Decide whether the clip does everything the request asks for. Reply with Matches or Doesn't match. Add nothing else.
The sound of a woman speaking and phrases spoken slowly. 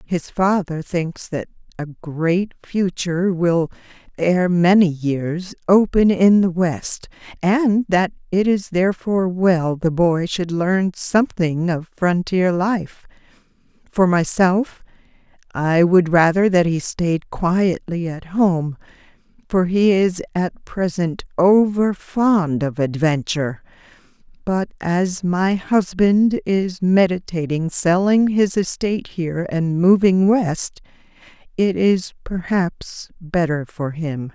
Matches